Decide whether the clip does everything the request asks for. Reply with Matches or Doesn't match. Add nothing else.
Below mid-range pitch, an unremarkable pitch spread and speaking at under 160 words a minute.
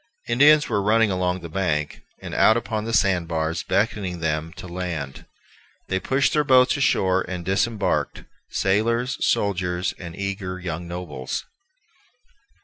Matches